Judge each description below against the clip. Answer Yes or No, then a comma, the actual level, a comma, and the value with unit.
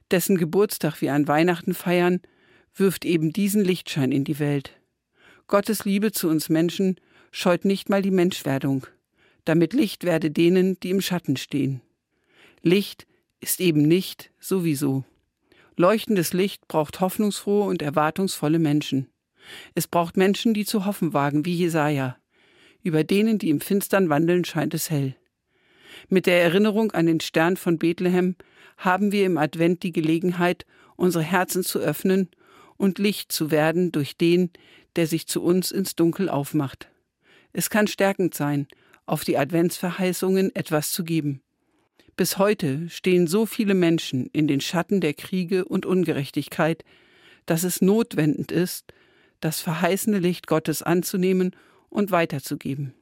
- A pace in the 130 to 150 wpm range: Yes, average, 145 wpm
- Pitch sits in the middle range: Yes, medium, 175 Hz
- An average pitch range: Yes, average, 3.6 semitones